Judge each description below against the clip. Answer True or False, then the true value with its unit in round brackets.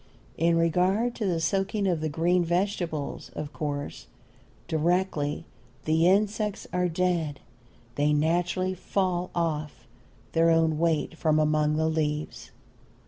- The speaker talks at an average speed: False (125 wpm)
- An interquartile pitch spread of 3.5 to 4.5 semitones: False (2.9 semitones)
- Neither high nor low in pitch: True (165 Hz)